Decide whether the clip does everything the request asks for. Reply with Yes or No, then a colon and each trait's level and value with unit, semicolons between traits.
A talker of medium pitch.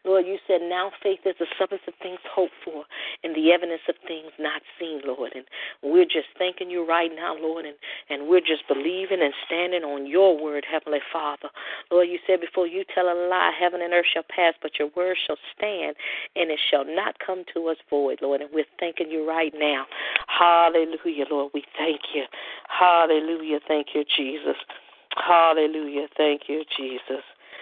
Yes: medium, 165 Hz